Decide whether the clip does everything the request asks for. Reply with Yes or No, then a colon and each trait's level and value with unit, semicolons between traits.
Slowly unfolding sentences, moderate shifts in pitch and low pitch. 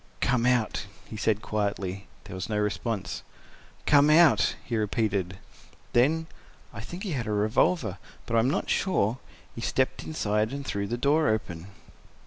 No: average, 145 wpm; average, 4.6 semitones; low, 110 Hz